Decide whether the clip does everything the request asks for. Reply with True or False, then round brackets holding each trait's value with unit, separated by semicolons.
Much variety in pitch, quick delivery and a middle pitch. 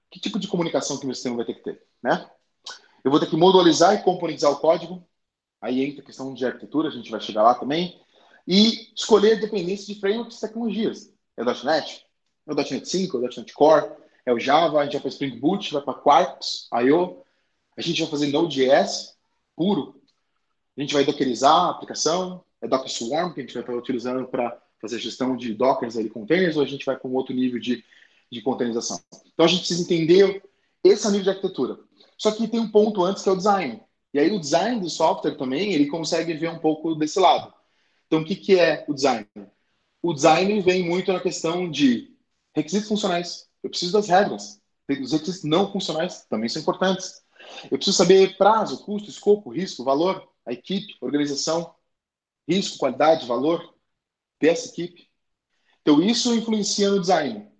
True (6.4 semitones; 195 wpm; 170 Hz)